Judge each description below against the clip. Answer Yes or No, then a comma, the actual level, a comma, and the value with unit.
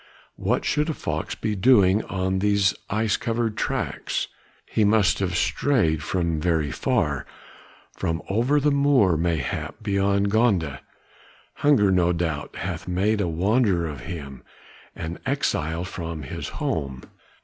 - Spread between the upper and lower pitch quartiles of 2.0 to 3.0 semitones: No, average, 4.9 semitones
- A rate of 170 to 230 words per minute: No, slow, 135 wpm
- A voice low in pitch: Yes, very low, 95 Hz